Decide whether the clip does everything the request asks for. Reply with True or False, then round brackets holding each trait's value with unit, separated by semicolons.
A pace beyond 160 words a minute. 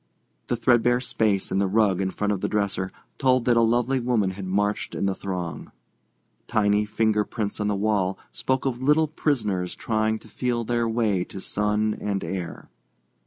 True (175 wpm)